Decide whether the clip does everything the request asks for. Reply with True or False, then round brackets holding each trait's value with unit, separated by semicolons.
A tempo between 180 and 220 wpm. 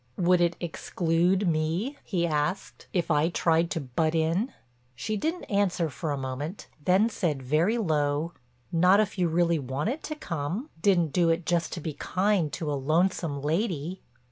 False (165 wpm)